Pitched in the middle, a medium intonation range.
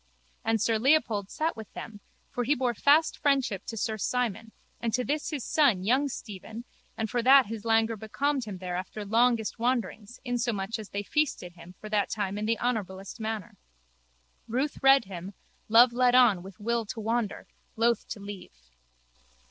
No: high, 225 Hz; average, 3.3 semitones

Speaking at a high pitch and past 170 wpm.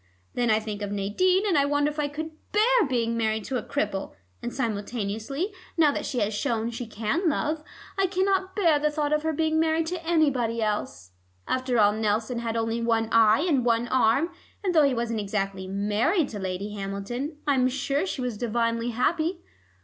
Yes: high, 245 Hz; average, 190 wpm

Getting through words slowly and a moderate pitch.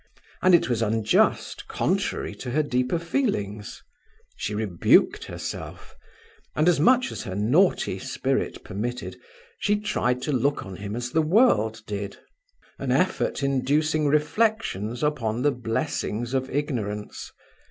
No: slow, 130 wpm; low, 125 Hz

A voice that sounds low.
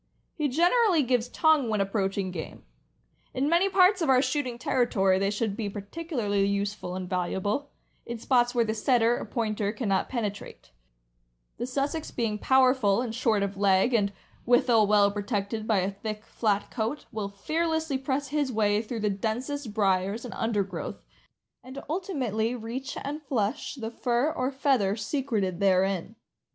No: high, 225 Hz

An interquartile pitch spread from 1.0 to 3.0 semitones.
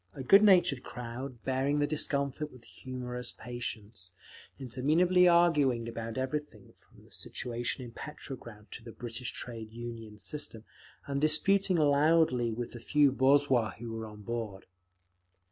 No: average, 4.0 semitones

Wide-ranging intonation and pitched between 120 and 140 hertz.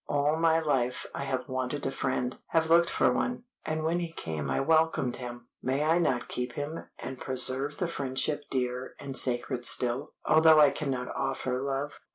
No: average, 3.7 semitones; low, 135 Hz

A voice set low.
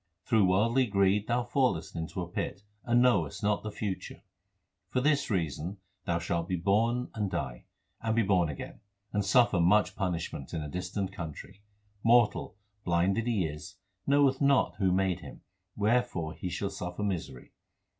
Yes: low, 100 Hz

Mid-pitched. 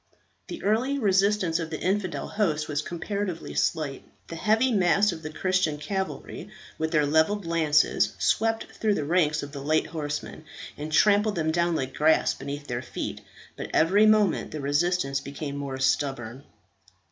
Yes: medium, 160 Hz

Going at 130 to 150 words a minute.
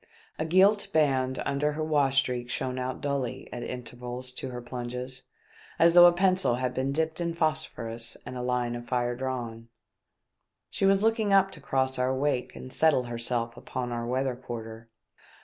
No: average, 175 wpm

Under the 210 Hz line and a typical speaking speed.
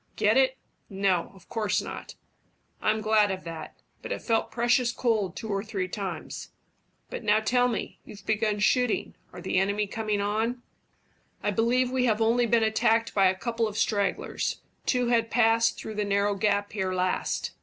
No: high, 215 Hz; average, 175 wpm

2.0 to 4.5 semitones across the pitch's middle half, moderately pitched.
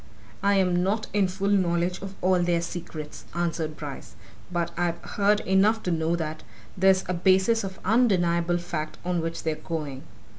Yes: narrow, 2.4 semitones; medium, 175 Hz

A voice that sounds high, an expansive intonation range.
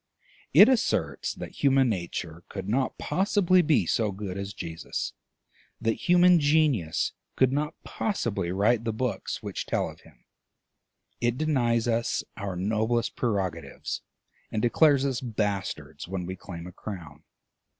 No: low, 110 Hz; wide, 6.1 semitones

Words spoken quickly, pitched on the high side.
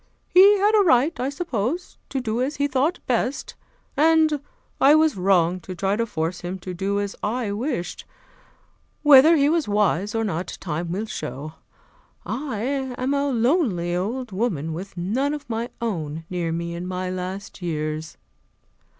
No: average, 165 wpm; high, 215 Hz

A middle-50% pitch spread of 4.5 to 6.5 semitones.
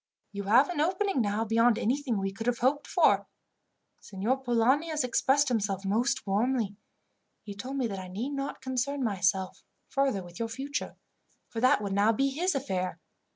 Yes: average, 5.2 semitones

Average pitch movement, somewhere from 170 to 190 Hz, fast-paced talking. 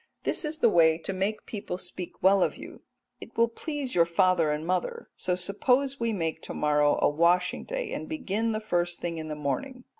No: wide, 5.7 semitones; medium, 185 Hz; fast, 215 wpm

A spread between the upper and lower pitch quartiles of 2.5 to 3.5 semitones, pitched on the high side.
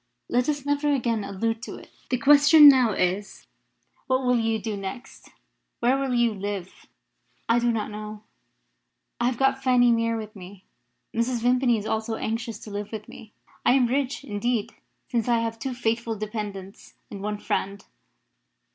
Yes: average, 3.0 semitones; high, 230 Hz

